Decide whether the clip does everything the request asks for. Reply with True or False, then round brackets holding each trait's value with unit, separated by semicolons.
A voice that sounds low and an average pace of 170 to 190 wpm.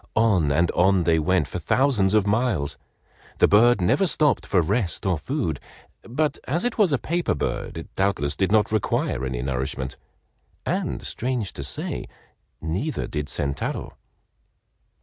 False (95 Hz; 150 wpm)